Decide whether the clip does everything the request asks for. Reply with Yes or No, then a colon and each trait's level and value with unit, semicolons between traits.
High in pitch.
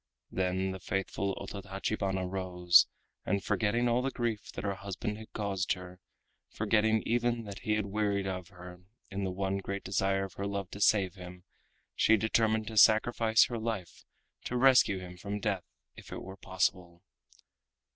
No: low, 100 Hz